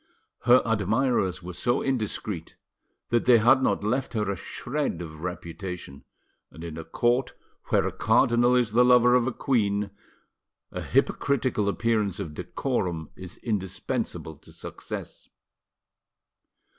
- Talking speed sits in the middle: No, slow, 130 wpm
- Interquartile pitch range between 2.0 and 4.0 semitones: No, average, 5.3 semitones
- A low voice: Yes, low, 110 Hz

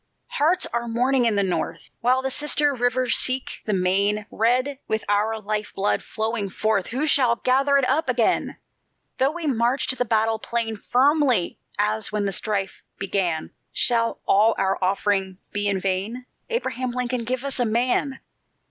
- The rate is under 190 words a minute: Yes, average, 165 wpm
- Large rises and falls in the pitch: No, average, 3.9 semitones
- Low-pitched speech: No, high, 230 Hz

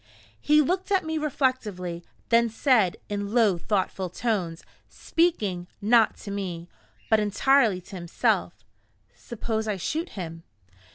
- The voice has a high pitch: Yes, high, 215 Hz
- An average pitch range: No, wide, 5.9 semitones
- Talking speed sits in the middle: No, slow, 125 wpm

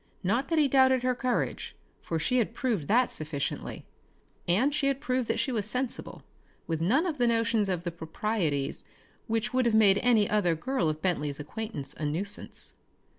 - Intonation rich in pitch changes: Yes, wide, 6.9 semitones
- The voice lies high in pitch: Yes, high, 220 Hz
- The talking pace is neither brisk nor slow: Yes, average, 180 wpm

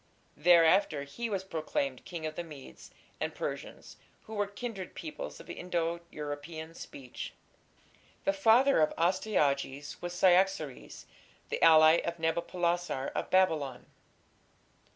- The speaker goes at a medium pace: No, slow, 120 wpm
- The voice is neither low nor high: Yes, medium, 170 Hz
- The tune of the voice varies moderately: Yes, average, 3.9 semitones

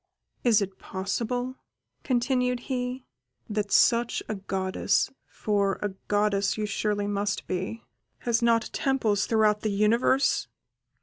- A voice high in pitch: Yes, high, 215 Hz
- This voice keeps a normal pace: No, slow, 120 wpm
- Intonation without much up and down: No, average, 3.2 semitones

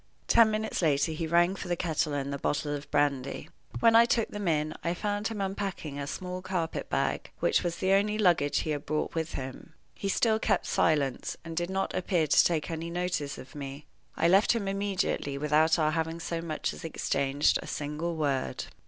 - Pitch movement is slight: No, average, 4.4 semitones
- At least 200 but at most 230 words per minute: Yes, fast, 205 wpm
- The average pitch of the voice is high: No, medium, 165 Hz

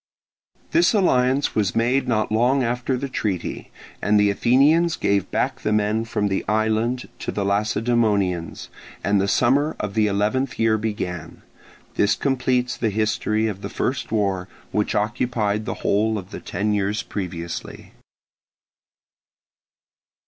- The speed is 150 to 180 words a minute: No, average, 140 wpm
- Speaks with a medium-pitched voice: No, low, 110 Hz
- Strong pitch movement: No, average, 3.4 semitones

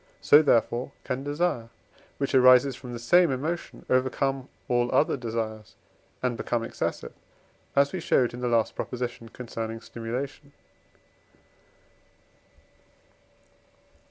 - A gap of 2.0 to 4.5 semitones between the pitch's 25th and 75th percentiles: Yes, average, 2.8 semitones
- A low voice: Yes, low, 125 Hz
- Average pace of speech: No, slow, 110 wpm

